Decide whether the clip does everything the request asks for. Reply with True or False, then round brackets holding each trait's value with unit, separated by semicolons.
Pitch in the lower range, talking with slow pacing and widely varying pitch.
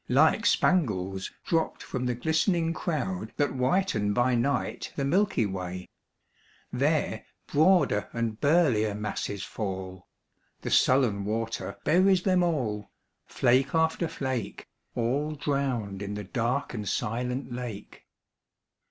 True (125 Hz; 125 wpm; 6.8 semitones)